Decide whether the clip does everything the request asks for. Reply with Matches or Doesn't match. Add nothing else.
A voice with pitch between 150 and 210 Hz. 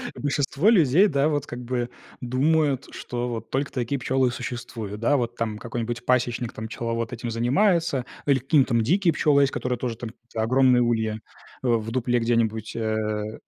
Doesn't match